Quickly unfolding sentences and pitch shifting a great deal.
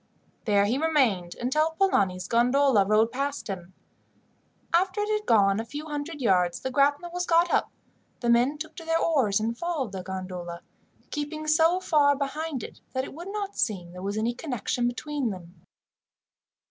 No: average, 170 wpm; wide, 7.6 semitones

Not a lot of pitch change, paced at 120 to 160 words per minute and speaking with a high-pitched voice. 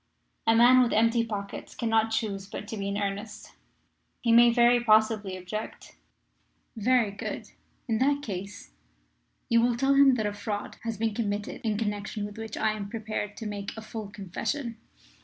No: narrow, 2.2 semitones; average, 170 wpm; high, 220 Hz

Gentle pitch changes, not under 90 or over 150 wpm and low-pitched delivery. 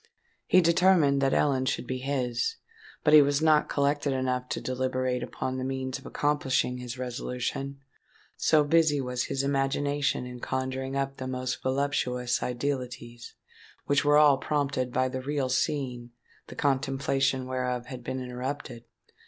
Yes: narrow, 2.0 semitones; average, 145 wpm; low, 130 Hz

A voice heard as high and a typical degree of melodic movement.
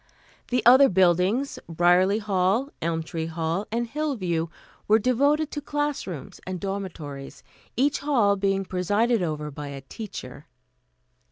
No: high, 195 Hz; wide, 6.6 semitones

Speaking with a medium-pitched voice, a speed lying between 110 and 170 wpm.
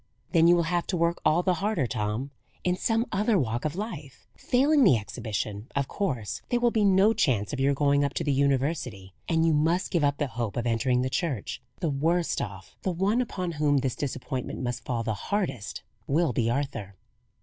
No: medium, 145 Hz; fast, 205 wpm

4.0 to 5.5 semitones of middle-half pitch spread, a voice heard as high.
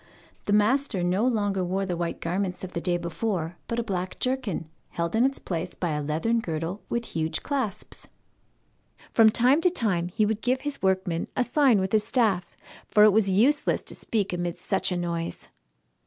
Yes: average, 4.8 semitones; high, 195 Hz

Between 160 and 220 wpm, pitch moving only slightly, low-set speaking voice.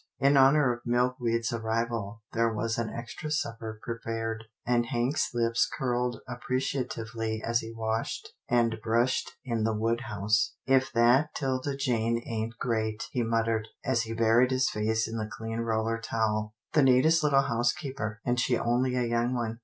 Yes: average, 175 wpm; narrow, 1.9 semitones; low, 115 Hz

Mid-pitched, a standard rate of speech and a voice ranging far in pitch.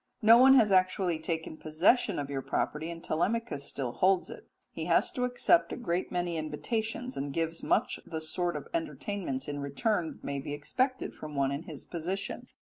Yes: medium, 170 Hz; average, 190 wpm; wide, 6.5 semitones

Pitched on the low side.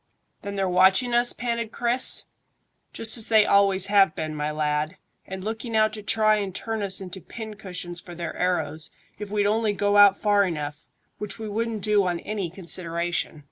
No: high, 200 Hz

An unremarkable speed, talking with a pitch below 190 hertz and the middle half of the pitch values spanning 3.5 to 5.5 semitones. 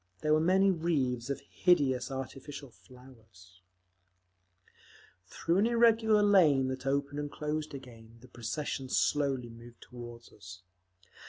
No: slow, 120 wpm; low, 135 Hz; average, 4.3 semitones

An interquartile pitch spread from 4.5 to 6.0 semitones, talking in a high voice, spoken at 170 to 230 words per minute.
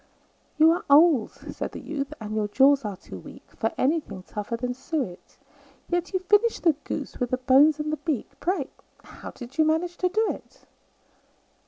Yes: average, 5.2 semitones; very high, 290 Hz; average, 185 wpm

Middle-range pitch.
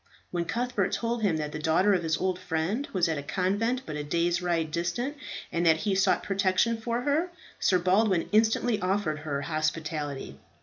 Yes: medium, 180 Hz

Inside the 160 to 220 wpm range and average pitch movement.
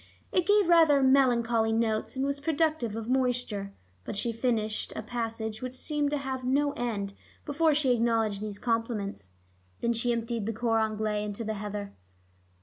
Yes: average, 165 wpm; average, 3.6 semitones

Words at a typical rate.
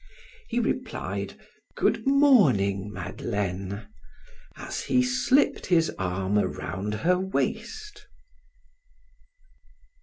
No: slow, 80 wpm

